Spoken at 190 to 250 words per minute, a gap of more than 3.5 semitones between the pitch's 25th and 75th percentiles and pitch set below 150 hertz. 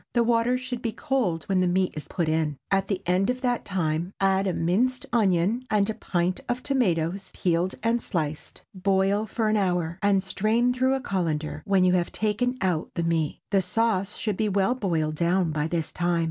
No: average, 200 wpm; average, 4.7 semitones; high, 190 Hz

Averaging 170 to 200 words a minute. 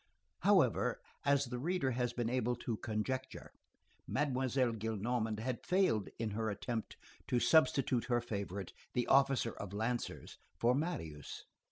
No: slow, 135 wpm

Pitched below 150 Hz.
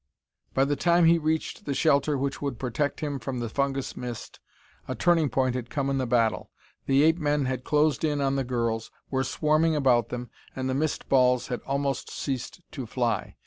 Yes: low, 135 Hz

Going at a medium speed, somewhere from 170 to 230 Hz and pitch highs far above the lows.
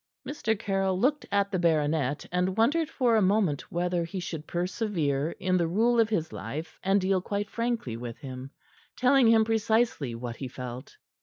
Yes: average, 175 wpm; medium, 185 Hz; wide, 6.6 semitones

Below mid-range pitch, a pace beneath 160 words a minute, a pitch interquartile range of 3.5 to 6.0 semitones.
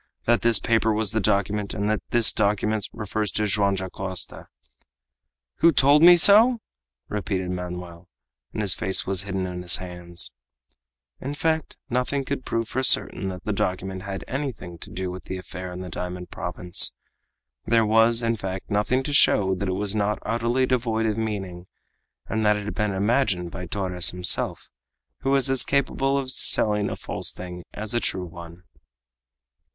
No: low, 105 Hz; average, 175 wpm; average, 4.1 semitones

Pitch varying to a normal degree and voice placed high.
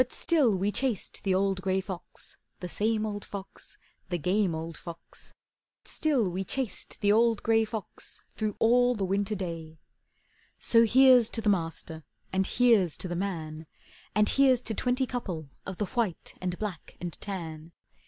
Yes: average, 4.4 semitones; high, 200 Hz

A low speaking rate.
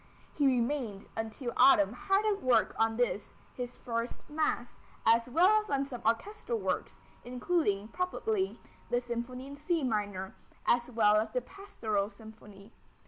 No: average, 145 wpm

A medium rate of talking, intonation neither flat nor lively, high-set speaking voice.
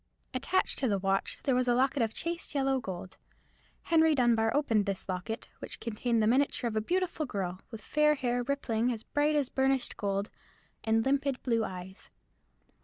Yes: average, 180 wpm; average, 4.6 semitones; high, 245 Hz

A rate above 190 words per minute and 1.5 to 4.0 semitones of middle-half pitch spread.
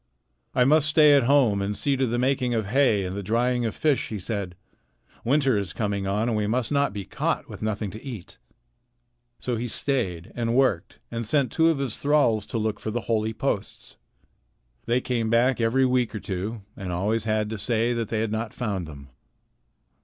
Yes: fast, 205 wpm; average, 3.5 semitones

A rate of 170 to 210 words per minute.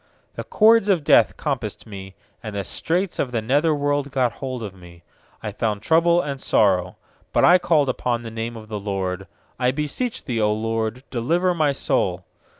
Yes: average, 185 wpm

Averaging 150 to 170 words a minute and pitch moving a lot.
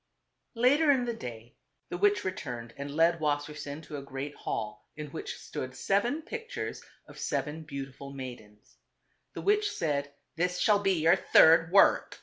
Yes: average, 155 wpm; wide, 6.6 semitones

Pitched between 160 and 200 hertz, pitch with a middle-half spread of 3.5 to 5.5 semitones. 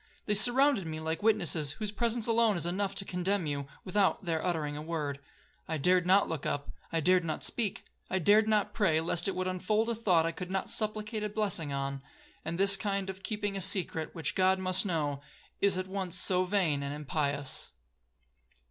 Yes: medium, 185 Hz; average, 4.2 semitones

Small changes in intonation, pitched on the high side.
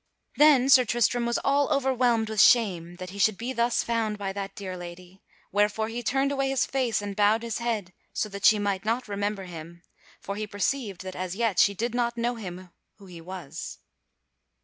No: average, 3.8 semitones; high, 210 Hz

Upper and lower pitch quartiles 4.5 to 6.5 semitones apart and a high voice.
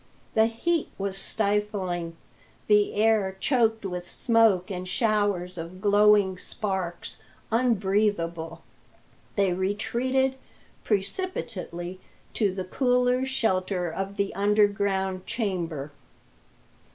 No: average, 3.1 semitones; high, 200 Hz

